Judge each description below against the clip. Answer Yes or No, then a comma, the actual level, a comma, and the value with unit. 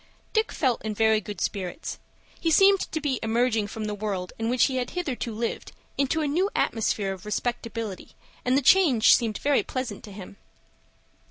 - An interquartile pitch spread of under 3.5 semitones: No, average, 4.8 semitones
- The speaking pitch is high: Yes, high, 230 Hz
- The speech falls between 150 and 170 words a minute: No, average, 180 wpm